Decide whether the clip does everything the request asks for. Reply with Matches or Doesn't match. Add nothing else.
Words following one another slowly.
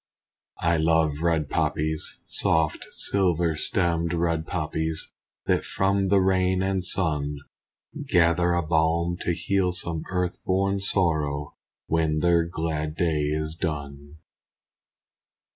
Matches